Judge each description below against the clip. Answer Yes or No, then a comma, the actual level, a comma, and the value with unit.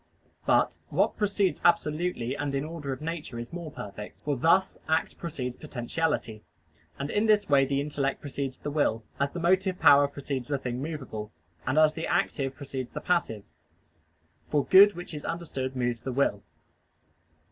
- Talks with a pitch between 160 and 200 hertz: No, medium, 145 Hz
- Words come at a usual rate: Yes, average, 170 wpm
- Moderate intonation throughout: Yes, average, 4.1 semitones